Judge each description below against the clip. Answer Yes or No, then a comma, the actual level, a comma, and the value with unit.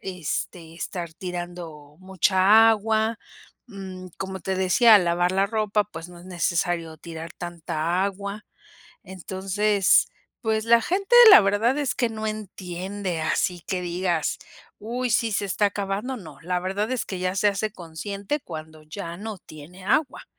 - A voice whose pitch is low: No, high, 190 Hz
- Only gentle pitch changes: No, average, 3.5 semitones